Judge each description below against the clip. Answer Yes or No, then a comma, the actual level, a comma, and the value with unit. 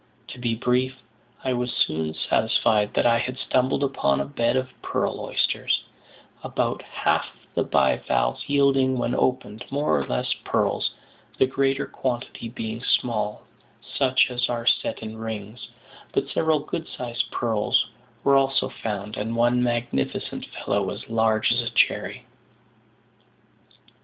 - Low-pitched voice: Yes, low, 120 Hz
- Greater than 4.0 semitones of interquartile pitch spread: No, average, 2.9 semitones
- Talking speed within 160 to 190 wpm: No, average, 140 wpm